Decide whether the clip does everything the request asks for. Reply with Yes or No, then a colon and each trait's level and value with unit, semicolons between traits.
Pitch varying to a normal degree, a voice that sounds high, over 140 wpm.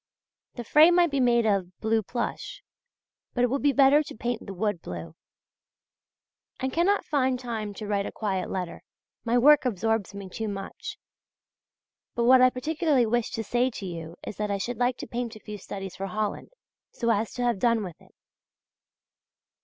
Yes: average, 4.0 semitones; high, 230 Hz; average, 185 wpm